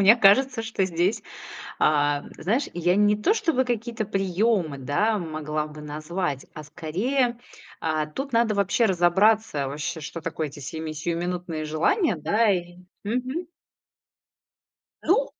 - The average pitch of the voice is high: No, medium, 180 Hz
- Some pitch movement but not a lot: No, wide, 6.4 semitones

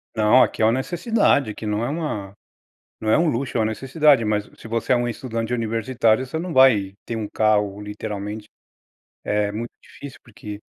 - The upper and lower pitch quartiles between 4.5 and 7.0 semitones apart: No, average, 3.7 semitones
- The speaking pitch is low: Yes, low, 115 Hz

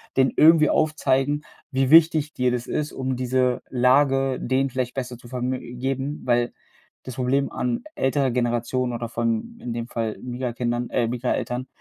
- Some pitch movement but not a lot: No, narrow, 1.8 semitones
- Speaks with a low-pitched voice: Yes, low, 125 Hz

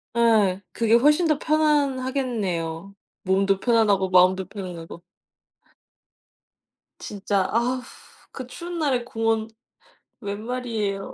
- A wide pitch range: No, average, 4.7 semitones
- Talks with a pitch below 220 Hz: No, high, 225 Hz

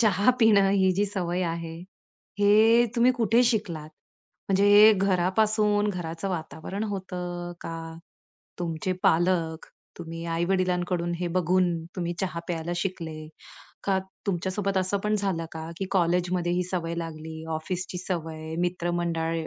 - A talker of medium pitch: Yes, medium, 180 Hz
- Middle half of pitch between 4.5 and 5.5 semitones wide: No, average, 2.8 semitones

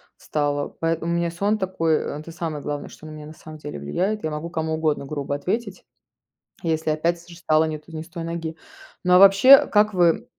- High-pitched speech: No, medium, 165 Hz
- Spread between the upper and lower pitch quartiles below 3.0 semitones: Yes, narrow, 2.4 semitones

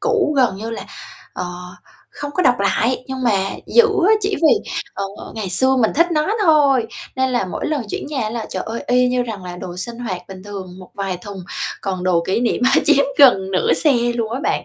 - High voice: Yes, high, 235 Hz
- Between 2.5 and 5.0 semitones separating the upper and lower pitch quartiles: No, wide, 5.6 semitones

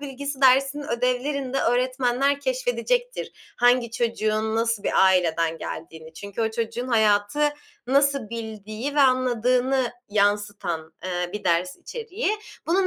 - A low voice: No, high, 240 Hz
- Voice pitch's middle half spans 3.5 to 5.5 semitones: Yes, average, 4.8 semitones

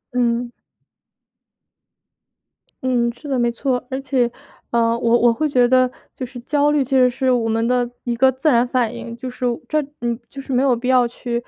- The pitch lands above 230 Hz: Yes, high, 245 Hz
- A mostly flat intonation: Yes, narrow, 1.7 semitones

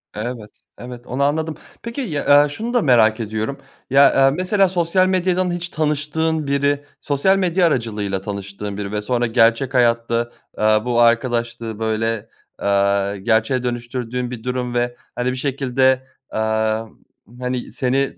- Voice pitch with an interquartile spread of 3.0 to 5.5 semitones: Yes, average, 4.3 semitones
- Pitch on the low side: Yes, low, 125 Hz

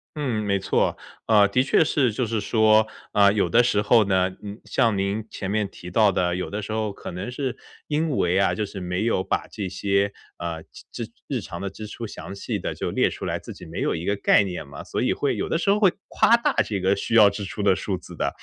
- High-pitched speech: No, low, 105 Hz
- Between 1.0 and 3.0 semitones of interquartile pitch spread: Yes, narrow, 2.6 semitones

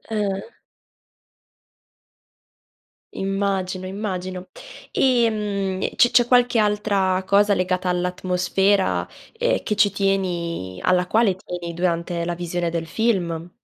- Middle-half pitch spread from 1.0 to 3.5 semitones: Yes, narrow, 2.5 semitones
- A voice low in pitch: No, medium, 185 Hz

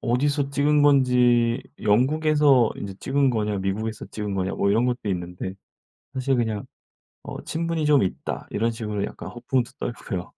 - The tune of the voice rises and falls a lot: No, average, 4.9 semitones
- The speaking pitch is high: No, low, 120 Hz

